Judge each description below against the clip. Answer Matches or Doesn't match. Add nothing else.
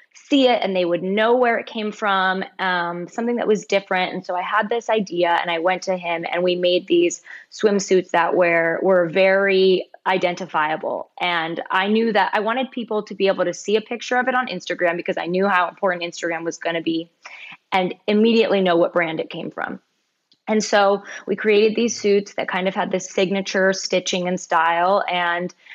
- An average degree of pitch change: Matches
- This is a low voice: Doesn't match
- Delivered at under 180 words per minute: Doesn't match